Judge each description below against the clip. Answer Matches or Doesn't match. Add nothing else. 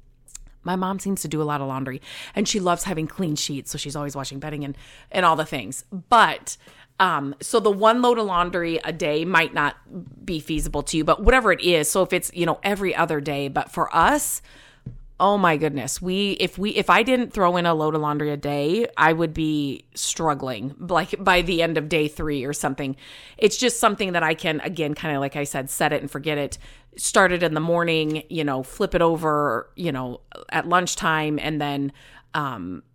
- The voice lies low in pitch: Doesn't match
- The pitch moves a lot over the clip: Doesn't match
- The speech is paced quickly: Matches